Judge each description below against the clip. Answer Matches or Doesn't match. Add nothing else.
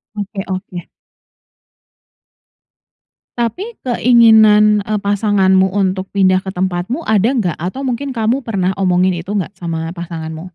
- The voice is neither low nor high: Doesn't match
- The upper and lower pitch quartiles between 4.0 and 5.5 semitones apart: Doesn't match